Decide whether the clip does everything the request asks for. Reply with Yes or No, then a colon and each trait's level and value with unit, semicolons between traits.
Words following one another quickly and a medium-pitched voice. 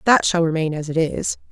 Yes: fast, 240 wpm; medium, 165 Hz